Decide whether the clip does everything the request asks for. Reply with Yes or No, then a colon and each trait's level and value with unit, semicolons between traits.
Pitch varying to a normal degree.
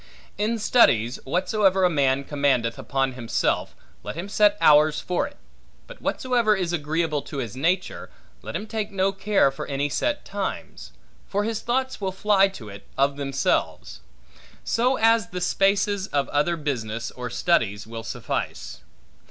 No: wide, 7.0 semitones